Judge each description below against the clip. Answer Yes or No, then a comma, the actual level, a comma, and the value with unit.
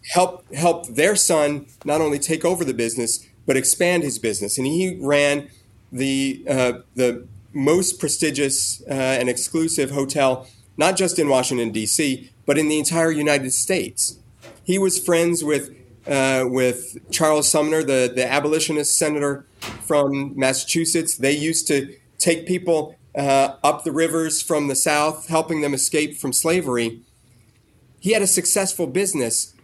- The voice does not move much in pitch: No, average, 4.1 semitones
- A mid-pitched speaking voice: Yes, medium, 145 Hz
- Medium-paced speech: Yes, average, 150 wpm